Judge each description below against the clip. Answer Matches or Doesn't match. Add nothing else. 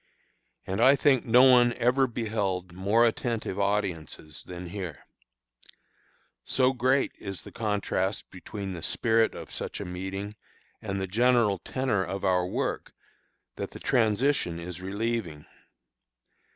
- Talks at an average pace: Doesn't match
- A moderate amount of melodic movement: Matches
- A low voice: Matches